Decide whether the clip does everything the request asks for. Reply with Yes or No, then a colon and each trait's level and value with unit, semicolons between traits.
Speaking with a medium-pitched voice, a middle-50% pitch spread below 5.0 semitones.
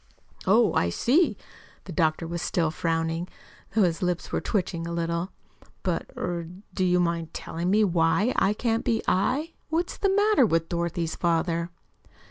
Yes: medium, 175 Hz; average, 4.3 semitones